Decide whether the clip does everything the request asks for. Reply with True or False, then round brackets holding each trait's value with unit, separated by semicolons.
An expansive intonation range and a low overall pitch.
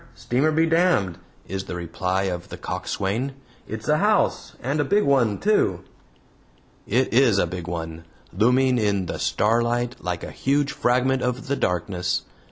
True (6.4 semitones; 120 Hz)